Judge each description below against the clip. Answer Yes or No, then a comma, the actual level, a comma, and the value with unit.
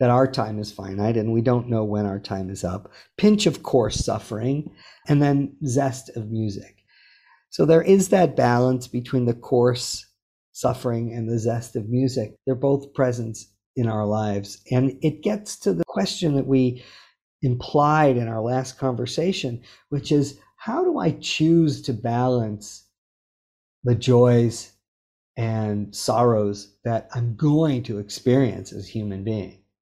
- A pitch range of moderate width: Yes, average, 4.6 semitones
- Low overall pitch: Yes, low, 120 Hz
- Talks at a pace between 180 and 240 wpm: No, average, 155 wpm